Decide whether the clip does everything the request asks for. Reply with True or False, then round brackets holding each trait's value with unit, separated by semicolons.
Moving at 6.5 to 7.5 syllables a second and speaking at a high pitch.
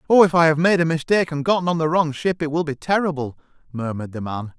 False (6.7 syllables/s; 155 Hz)